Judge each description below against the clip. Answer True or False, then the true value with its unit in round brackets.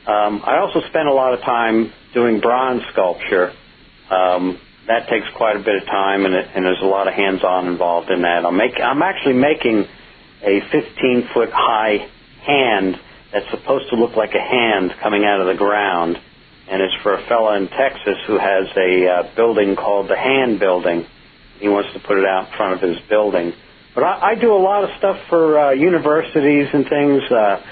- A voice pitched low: True (105 Hz)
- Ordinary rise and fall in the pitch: False (5.8 semitones)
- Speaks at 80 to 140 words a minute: False (195 wpm)